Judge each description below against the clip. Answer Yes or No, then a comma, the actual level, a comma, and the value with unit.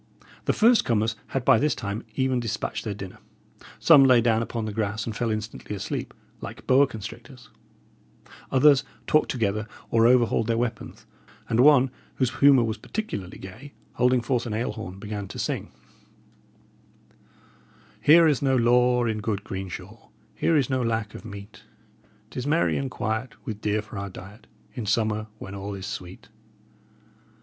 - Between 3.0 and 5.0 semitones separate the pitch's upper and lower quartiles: Yes, average, 3.4 semitones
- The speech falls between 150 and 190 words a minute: Yes, average, 165 wpm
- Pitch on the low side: Yes, low, 115 Hz